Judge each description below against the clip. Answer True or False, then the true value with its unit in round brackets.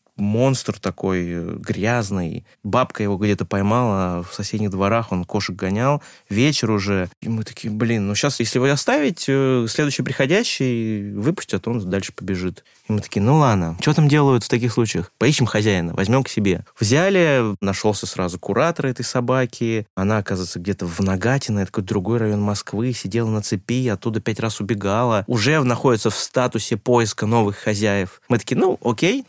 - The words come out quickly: True (165 wpm)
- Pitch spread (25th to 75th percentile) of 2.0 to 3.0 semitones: False (3.7 semitones)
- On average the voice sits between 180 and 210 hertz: False (110 Hz)